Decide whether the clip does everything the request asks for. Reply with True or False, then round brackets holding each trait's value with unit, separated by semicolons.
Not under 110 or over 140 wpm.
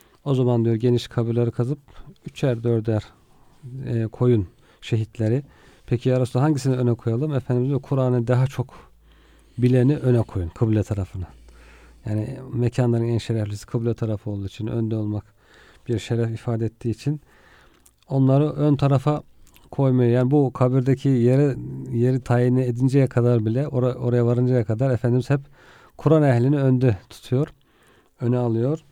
True (135 wpm)